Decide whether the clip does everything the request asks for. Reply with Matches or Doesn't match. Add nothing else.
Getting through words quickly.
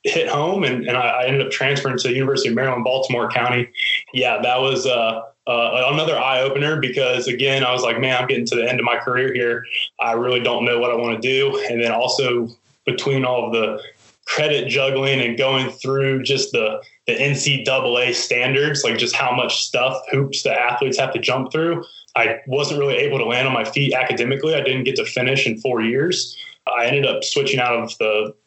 Matches